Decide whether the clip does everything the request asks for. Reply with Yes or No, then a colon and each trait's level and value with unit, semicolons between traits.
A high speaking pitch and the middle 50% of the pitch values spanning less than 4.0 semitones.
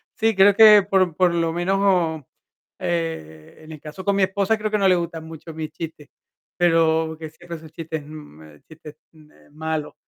No: medium, 165 Hz; average, 3.2 semitones